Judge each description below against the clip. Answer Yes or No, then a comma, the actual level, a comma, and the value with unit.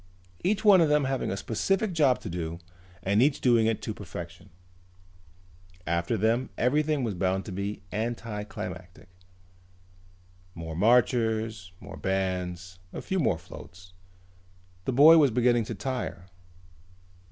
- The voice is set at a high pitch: No, low, 110 Hz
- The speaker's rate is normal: No, slow, 130 wpm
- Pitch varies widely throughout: Yes, wide, 5.9 semitones